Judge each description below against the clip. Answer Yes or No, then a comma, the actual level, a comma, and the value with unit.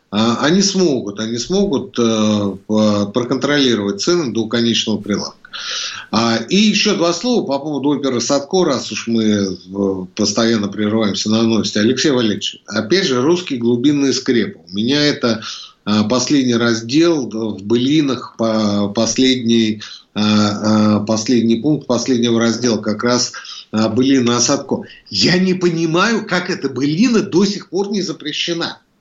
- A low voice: Yes, low, 120 Hz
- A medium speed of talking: Yes, average, 120 wpm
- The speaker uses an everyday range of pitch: No, wide, 5.8 semitones